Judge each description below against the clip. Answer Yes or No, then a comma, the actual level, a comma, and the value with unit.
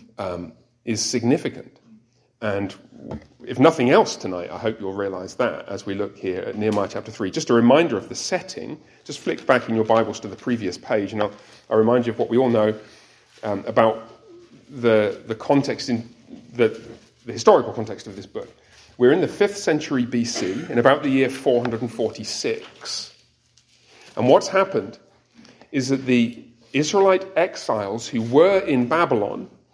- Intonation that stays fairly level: No, average, 3.6 semitones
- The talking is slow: No, average, 165 wpm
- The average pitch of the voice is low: Yes, low, 120 Hz